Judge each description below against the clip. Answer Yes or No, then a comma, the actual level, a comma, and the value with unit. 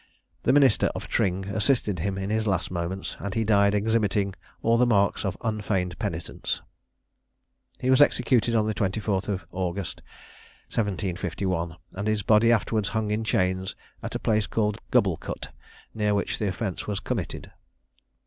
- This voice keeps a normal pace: Yes, average, 155 wpm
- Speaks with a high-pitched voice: No, low, 105 Hz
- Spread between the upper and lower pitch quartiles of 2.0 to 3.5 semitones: Yes, narrow, 2.6 semitones